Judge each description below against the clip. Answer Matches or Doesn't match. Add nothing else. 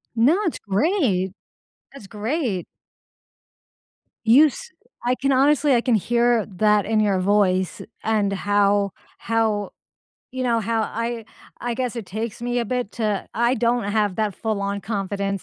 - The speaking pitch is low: Doesn't match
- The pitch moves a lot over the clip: Doesn't match